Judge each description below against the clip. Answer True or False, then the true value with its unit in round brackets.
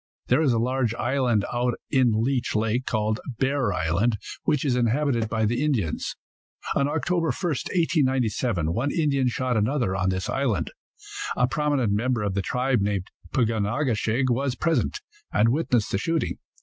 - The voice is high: False (125 Hz)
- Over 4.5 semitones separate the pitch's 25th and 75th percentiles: False (4.2 semitones)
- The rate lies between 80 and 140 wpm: False (170 wpm)